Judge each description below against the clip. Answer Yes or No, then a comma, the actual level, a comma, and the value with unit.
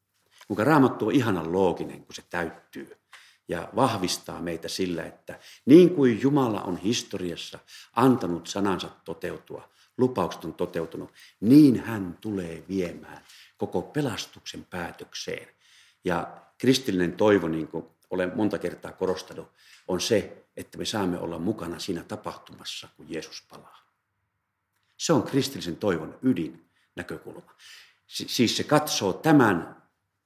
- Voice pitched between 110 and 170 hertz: No, very low, 95 Hz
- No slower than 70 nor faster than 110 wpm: No, average, 125 wpm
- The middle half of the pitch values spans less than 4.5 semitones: No, average, 5.2 semitones